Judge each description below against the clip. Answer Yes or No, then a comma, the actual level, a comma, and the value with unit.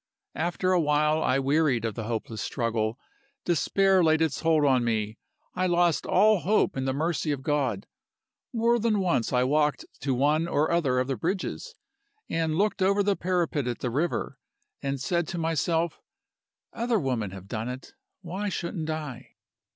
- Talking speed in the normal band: Yes, average, 170 wpm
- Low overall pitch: No, medium, 155 Hz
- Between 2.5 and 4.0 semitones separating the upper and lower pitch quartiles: No, wide, 5.4 semitones